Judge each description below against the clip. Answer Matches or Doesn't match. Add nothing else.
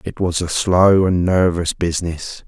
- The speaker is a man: Matches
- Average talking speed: Matches